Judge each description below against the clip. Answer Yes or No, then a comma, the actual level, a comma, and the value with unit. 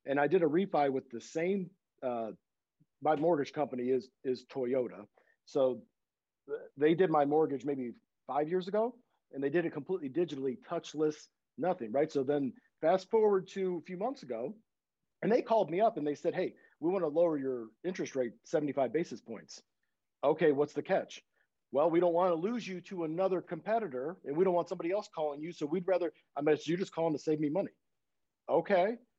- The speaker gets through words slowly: No, average, 200 wpm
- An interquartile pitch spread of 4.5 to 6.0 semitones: Yes, average, 4.8 semitones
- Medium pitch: Yes, medium, 160 Hz